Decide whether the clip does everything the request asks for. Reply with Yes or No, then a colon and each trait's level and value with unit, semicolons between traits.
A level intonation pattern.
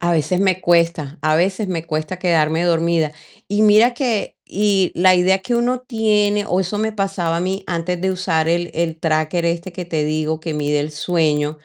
No: average, 3.4 semitones